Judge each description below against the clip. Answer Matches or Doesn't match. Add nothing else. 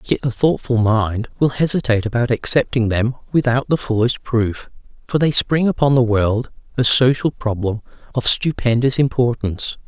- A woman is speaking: Doesn't match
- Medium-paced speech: Matches